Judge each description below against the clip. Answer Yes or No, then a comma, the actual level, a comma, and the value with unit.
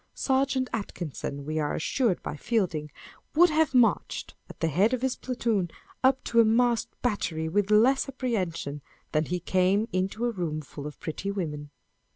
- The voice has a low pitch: No, high, 200 Hz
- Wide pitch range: Yes, wide, 7.3 semitones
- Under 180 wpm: Yes, average, 170 wpm